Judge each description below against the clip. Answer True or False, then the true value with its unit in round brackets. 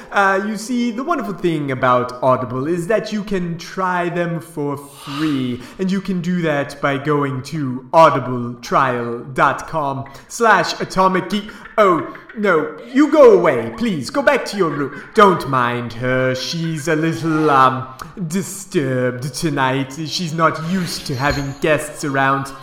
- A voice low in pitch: False (160 Hz)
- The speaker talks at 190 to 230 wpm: False (140 wpm)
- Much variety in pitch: True (5.7 semitones)